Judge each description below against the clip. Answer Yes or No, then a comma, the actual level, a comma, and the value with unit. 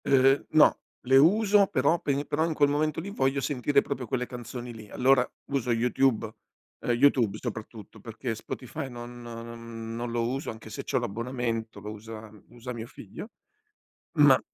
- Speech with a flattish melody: No, average, 3.2 semitones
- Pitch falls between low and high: No, low, 125 Hz